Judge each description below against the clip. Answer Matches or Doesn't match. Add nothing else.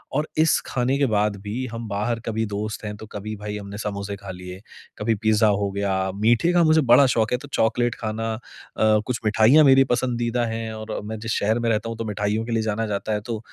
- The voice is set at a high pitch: Doesn't match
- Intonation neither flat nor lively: Doesn't match